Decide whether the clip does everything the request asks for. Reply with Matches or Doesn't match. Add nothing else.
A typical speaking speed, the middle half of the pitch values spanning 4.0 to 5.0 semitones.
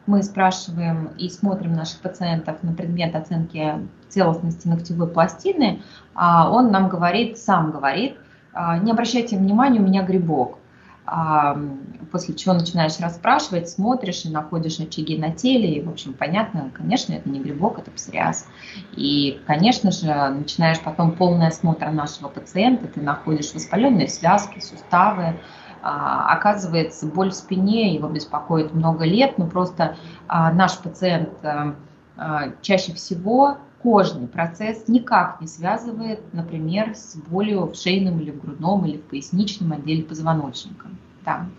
Doesn't match